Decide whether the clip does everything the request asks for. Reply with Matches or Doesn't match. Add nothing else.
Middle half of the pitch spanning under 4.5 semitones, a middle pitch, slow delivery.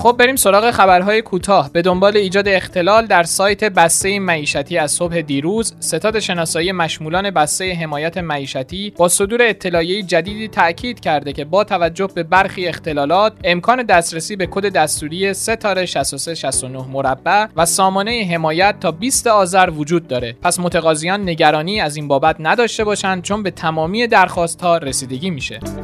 Doesn't match